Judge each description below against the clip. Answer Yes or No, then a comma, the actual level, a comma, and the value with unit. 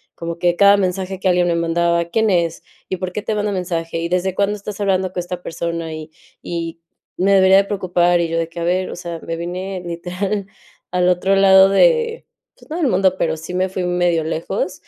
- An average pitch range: No, narrow, 2.3 semitones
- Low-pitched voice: No, medium, 180 Hz